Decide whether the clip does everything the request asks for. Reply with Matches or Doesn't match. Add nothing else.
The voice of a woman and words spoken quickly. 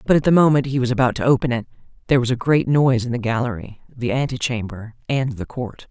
Matches